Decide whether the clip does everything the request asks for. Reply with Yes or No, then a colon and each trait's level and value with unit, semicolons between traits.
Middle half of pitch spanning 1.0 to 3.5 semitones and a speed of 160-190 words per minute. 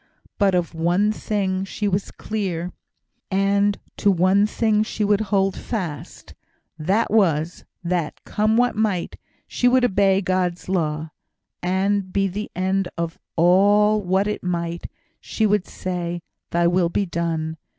No: average, 2.9 semitones; average, 140 wpm